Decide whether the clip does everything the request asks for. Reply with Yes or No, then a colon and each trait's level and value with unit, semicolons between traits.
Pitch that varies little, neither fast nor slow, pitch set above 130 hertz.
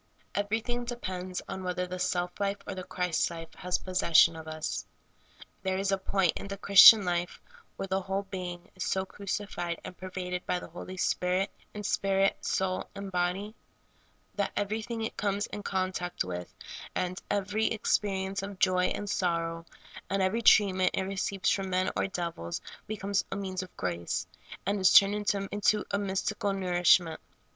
Yes: narrow, 1.8 semitones; average, 170 wpm; high, 190 Hz